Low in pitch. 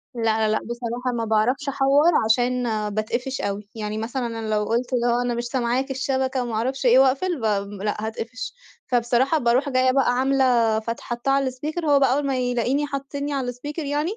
No: very high, 250 Hz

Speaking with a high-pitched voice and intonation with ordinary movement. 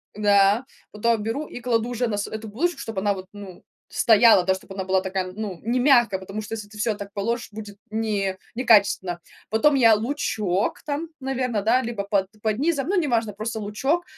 Yes: high, 220 Hz; average, 3.2 semitones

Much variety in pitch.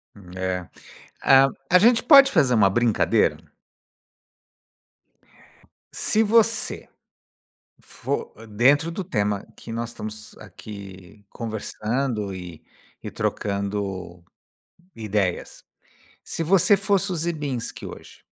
Yes: wide, 8.9 semitones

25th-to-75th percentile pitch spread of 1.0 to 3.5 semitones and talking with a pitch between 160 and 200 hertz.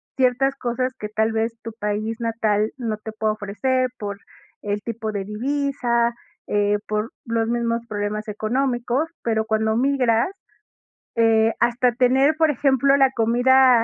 No: average, 2.9 semitones; high, 230 Hz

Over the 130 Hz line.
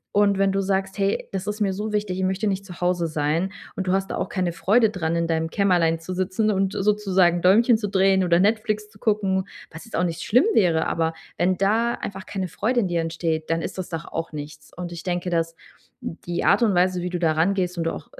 Yes: medium, 185 Hz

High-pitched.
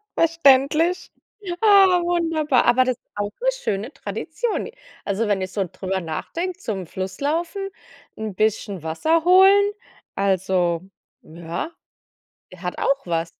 Yes: very high, 250 Hz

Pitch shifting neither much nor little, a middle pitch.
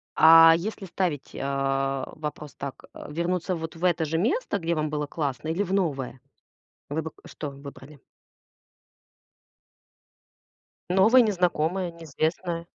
Yes: average, 3.5 semitones; medium, 160 Hz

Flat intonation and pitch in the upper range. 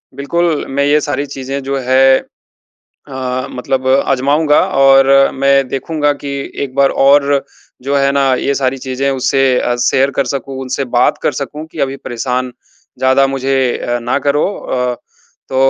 No: narrow, 1.2 semitones; low, 135 Hz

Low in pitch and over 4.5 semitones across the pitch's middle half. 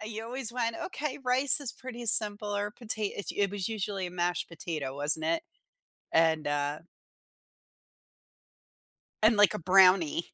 No: high, 205 Hz; wide, 5.4 semitones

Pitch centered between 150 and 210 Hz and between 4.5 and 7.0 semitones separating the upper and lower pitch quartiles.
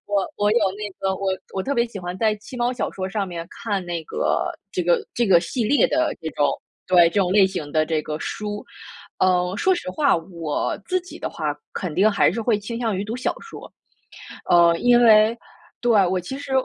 Yes: high, 200 Hz; average, 4.8 semitones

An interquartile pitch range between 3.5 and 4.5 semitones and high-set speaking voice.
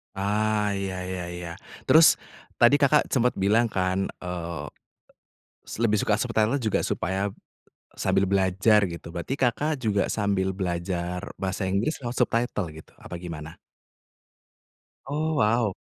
No: average, 4.1 semitones; low, 100 Hz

